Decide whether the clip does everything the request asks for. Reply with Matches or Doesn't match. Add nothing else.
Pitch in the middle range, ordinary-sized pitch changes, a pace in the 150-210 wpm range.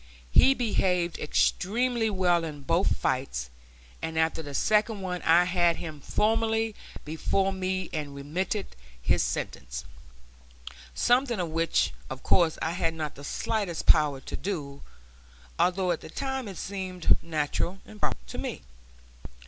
Doesn't match